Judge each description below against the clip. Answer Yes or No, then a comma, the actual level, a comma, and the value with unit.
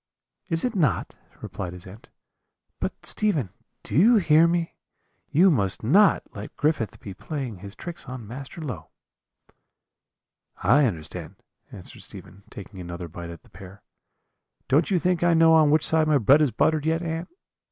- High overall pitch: No, medium, 140 Hz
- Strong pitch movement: Yes, wide, 8.7 semitones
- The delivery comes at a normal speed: Yes, average, 165 wpm